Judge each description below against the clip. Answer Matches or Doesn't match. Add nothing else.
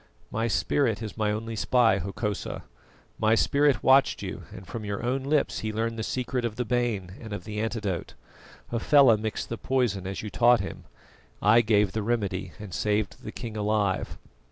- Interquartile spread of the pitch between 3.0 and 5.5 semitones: Doesn't match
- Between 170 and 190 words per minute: Matches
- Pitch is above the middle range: Doesn't match